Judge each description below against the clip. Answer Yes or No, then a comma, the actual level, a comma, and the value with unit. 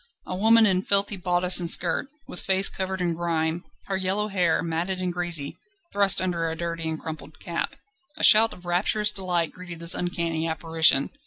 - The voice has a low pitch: No, medium, 175 Hz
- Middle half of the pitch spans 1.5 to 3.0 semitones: Yes, narrow, 2.4 semitones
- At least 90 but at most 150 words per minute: No, average, 180 wpm